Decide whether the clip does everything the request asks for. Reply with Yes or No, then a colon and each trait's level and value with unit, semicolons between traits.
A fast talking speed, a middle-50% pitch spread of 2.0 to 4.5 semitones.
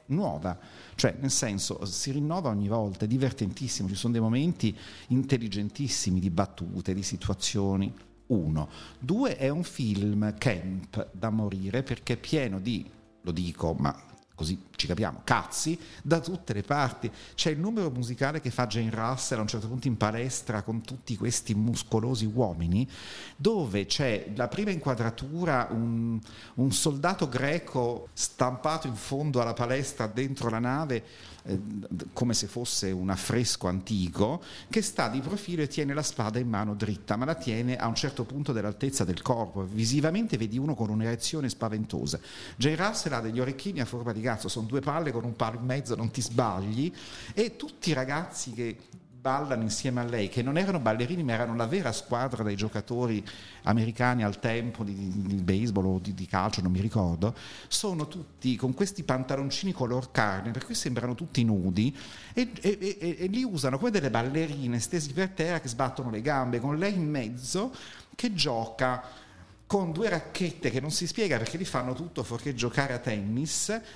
No: fast, 175 wpm; average, 5.1 semitones